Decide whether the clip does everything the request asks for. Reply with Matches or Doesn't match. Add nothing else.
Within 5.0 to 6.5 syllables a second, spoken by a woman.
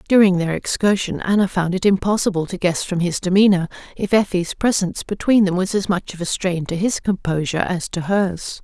Matches